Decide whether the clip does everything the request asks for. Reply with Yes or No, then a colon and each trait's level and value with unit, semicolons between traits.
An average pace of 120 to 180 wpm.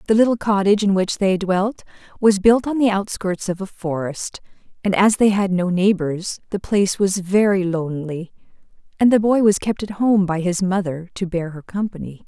No: average, 195 wpm